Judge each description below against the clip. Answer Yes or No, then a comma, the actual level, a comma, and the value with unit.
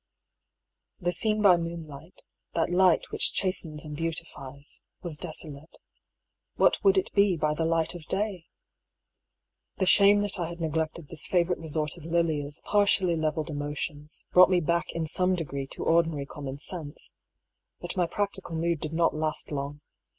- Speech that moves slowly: No, average, 165 wpm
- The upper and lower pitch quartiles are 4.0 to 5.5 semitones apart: No, average, 2.9 semitones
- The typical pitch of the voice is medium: Yes, medium, 165 Hz